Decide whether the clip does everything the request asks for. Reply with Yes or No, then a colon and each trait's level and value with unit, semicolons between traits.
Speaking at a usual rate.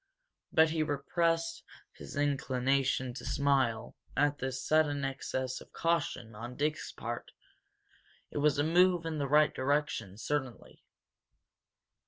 No: slow, 125 wpm